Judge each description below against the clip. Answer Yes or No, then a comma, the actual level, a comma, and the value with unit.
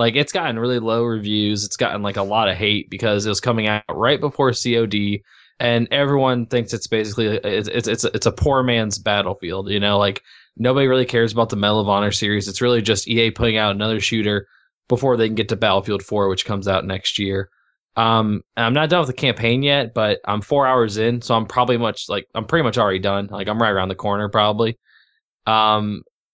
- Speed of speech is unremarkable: No, fast, 225 wpm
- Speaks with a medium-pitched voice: No, low, 110 Hz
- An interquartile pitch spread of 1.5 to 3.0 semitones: Yes, average, 2.7 semitones